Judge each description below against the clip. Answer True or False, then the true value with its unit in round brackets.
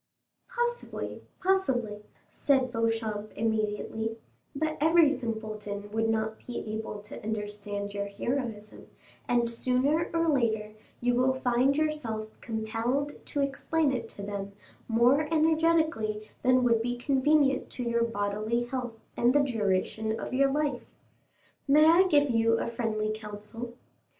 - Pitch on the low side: False (235 Hz)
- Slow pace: True (130 wpm)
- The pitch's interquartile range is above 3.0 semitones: True (4.3 semitones)